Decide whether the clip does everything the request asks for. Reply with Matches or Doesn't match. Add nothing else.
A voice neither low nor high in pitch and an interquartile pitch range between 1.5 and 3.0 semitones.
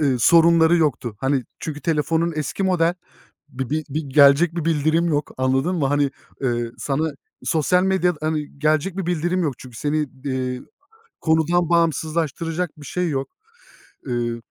Doesn't match